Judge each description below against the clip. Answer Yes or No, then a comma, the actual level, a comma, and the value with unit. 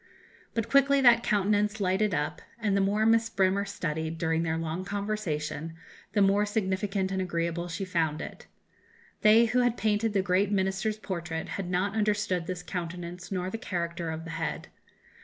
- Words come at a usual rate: Yes, average, 170 wpm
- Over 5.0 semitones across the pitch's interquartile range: No, average, 3.6 semitones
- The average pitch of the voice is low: No, high, 190 Hz